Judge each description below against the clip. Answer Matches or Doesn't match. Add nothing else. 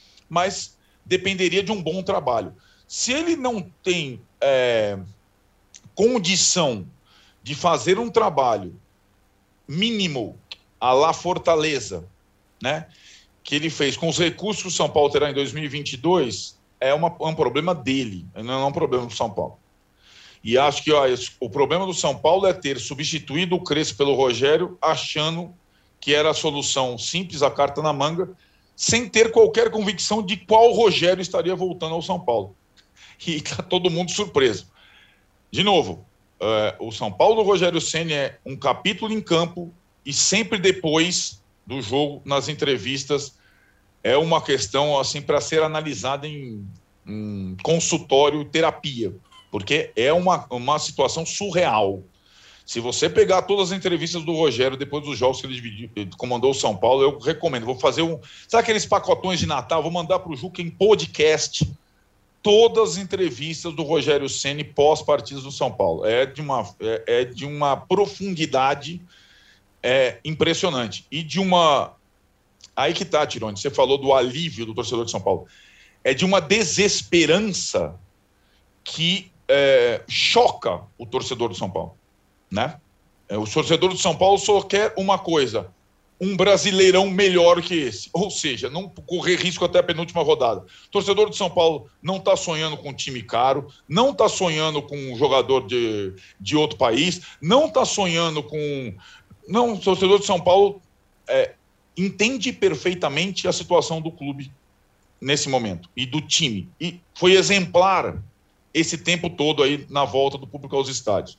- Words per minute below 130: Doesn't match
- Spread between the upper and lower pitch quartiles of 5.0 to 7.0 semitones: Matches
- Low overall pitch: Doesn't match